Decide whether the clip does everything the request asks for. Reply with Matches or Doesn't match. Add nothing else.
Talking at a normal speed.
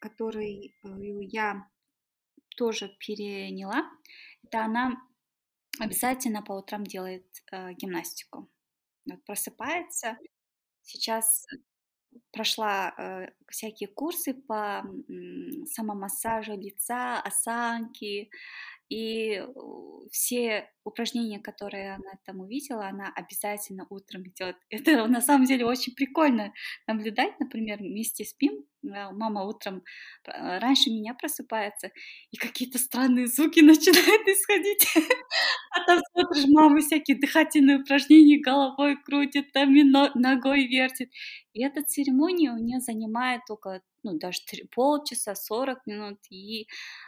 Doesn't match